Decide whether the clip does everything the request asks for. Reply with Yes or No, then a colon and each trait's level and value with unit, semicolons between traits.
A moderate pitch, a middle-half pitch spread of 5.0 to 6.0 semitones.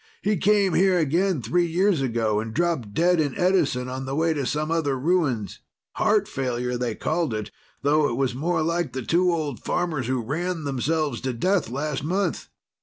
Yes: medium, 150 Hz; wide, 5.4 semitones